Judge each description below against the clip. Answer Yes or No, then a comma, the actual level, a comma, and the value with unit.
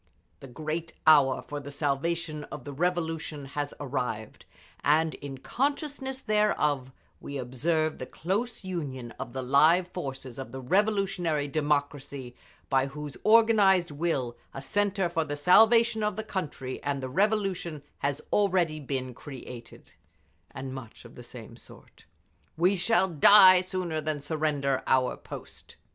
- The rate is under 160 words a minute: Yes, average, 140 wpm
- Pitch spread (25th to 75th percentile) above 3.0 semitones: Yes, wide, 5.4 semitones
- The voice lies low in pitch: No, medium, 155 Hz